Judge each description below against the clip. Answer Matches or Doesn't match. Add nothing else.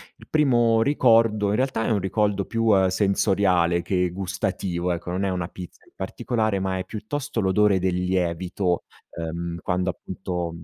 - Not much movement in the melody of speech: Doesn't match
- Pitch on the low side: Matches